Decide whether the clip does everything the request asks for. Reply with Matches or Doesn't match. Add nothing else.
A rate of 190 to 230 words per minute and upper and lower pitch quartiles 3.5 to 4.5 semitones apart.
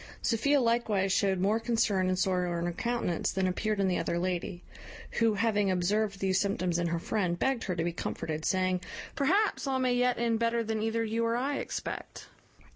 Matches